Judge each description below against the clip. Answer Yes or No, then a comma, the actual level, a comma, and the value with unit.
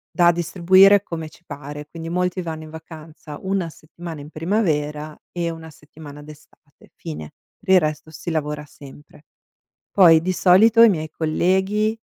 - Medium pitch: Yes, medium, 160 Hz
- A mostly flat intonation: No, average, 3.0 semitones